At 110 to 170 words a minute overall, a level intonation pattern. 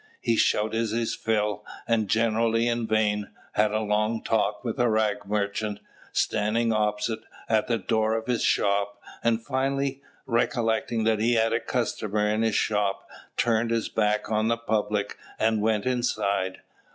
Yes: average, 155 wpm; narrow, 1.6 semitones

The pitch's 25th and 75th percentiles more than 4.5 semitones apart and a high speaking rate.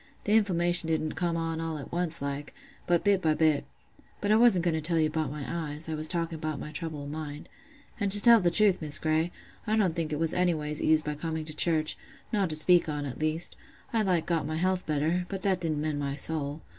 No: narrow, 2.5 semitones; fast, 230 wpm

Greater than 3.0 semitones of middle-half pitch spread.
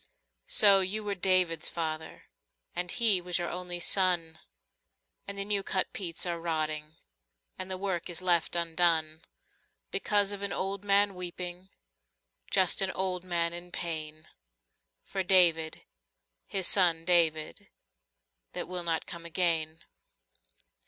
No: narrow, 2.4 semitones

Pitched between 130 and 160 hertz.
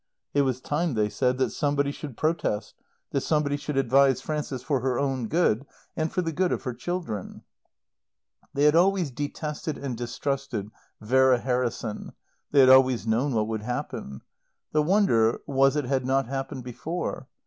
Yes: low, 135 Hz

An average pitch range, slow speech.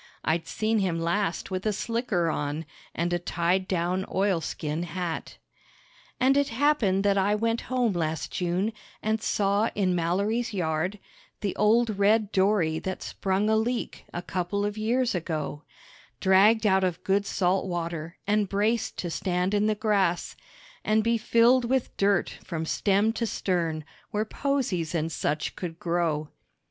No: average, 3.9 semitones; average, 155 wpm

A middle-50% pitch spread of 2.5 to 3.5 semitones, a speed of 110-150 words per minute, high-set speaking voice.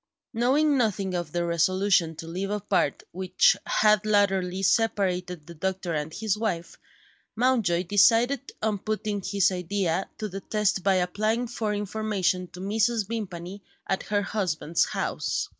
Yes: average, 3.1 semitones; average, 140 wpm; high, 195 Hz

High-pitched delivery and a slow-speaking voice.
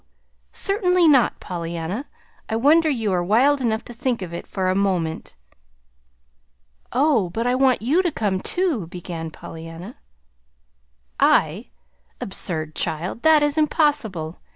Yes: high, 220 Hz; slow, 130 wpm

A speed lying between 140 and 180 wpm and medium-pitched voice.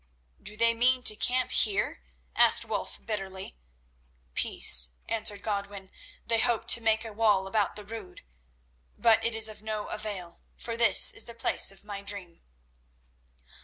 No: average, 155 wpm; high, 215 Hz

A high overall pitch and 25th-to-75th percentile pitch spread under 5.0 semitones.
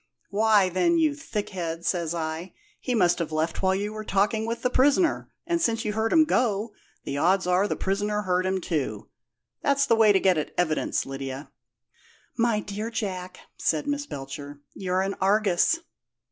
Yes: high, 195 Hz; average, 4.4 semitones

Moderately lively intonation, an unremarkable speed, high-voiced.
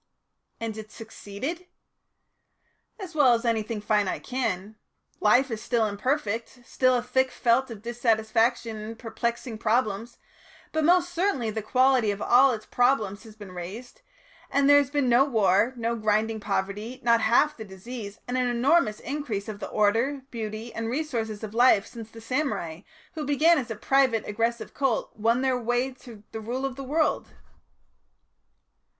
Yes: average, 3.3 semitones; average, 165 wpm; high, 235 Hz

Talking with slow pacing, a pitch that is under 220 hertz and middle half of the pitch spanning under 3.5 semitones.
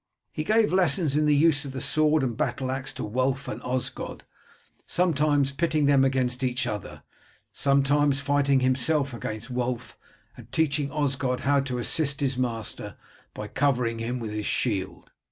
No: average, 160 wpm; low, 135 Hz; average, 2.7 semitones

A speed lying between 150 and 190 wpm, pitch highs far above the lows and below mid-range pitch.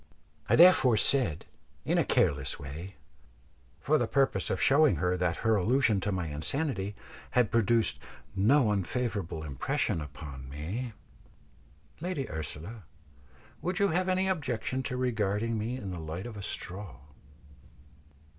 No: slow, 135 wpm; wide, 7.0 semitones; low, 110 Hz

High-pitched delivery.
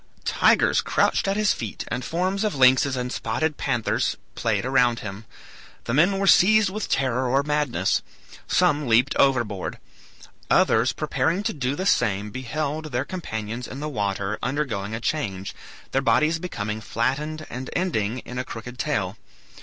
No: low, 130 Hz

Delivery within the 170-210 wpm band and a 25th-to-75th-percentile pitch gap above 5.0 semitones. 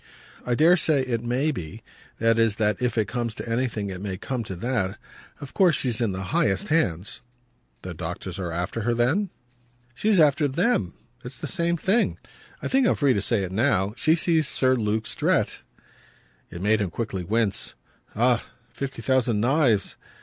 Yes: average, 180 wpm; wide, 5.4 semitones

